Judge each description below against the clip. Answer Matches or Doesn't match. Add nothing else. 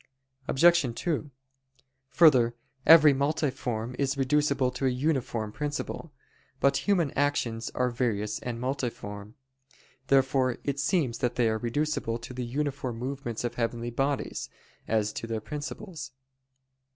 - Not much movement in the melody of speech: Doesn't match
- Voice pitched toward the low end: Matches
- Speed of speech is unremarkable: Doesn't match